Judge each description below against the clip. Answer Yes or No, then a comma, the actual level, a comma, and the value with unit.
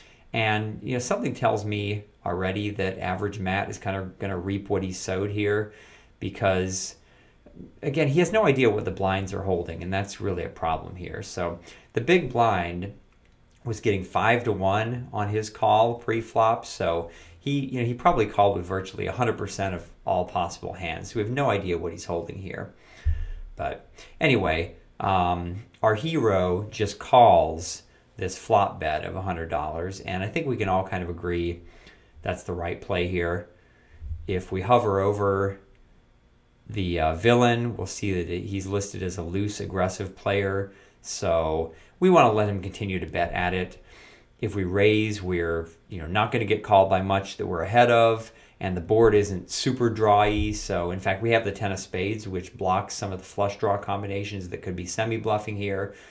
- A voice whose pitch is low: Yes, low, 100 Hz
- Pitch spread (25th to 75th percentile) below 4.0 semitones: Yes, average, 3.1 semitones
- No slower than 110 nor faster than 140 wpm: No, average, 185 wpm